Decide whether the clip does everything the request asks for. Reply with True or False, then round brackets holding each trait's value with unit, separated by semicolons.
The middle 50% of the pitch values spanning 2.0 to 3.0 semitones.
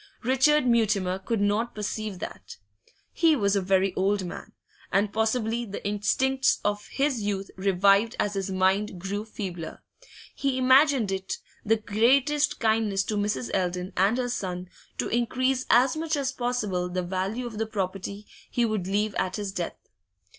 False (3.9 semitones)